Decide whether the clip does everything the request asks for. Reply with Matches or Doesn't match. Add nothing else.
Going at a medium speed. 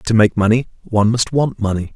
Doesn't match